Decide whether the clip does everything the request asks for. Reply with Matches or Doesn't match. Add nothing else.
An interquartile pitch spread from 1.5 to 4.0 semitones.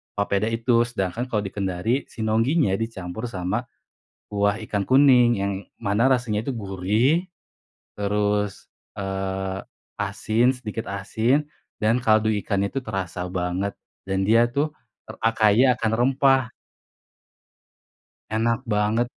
Matches